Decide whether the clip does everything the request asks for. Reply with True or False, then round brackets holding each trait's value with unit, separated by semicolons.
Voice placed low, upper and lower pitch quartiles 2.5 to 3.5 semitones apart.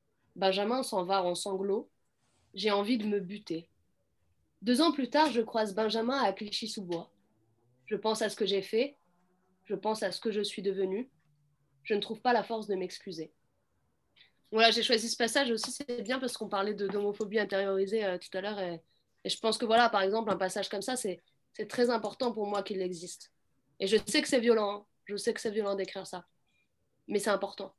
False (205 Hz; 2.9 semitones)